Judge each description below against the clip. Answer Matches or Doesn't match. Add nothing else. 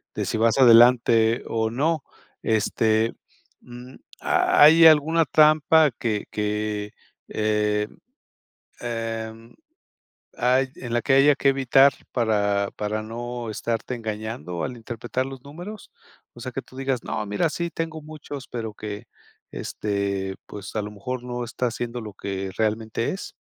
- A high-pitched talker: Doesn't match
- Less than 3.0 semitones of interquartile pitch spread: Doesn't match